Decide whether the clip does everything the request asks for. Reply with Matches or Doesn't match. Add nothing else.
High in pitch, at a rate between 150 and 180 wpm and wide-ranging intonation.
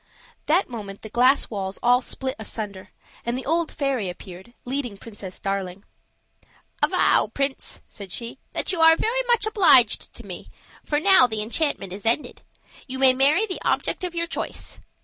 Matches